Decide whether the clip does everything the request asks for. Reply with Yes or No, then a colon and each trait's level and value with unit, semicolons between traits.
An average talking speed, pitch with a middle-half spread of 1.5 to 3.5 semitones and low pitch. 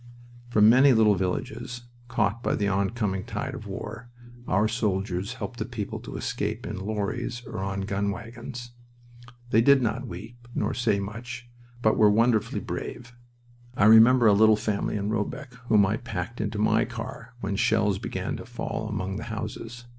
Yes: average, 170 wpm; average, 3.0 semitones; low, 110 Hz